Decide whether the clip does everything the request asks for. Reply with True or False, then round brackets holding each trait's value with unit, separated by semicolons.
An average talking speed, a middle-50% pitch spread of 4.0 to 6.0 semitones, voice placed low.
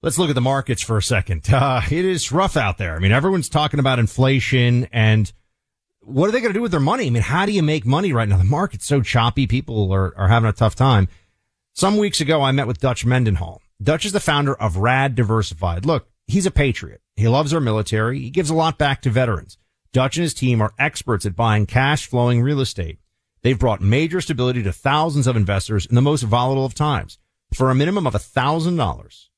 False (230 wpm; 5.3 semitones; 125 Hz)